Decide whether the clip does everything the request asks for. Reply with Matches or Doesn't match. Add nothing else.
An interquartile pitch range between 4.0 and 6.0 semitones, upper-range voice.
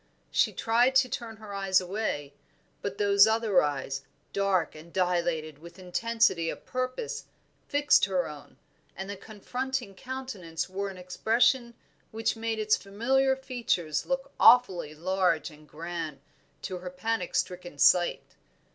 Matches